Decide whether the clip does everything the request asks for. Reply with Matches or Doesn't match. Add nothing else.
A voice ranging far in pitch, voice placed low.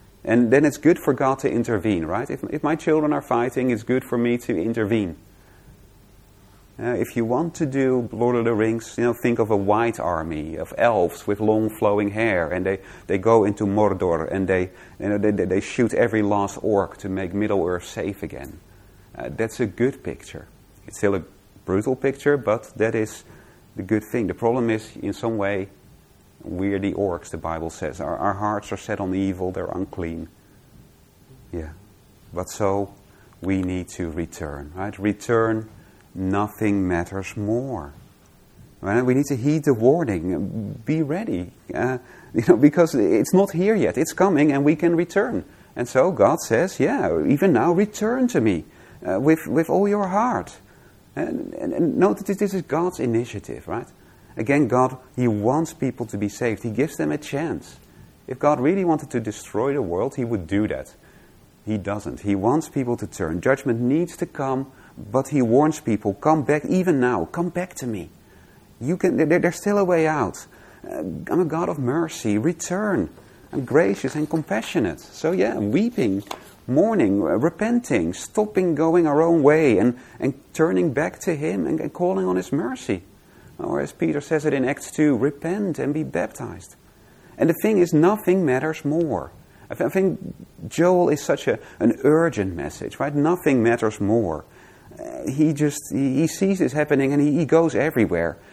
Matches